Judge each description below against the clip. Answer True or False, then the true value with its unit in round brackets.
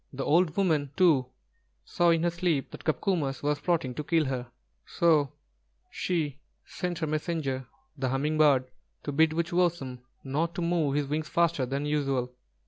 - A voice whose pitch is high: False (150 Hz)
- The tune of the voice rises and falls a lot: False (3.6 semitones)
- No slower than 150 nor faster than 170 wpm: True (160 wpm)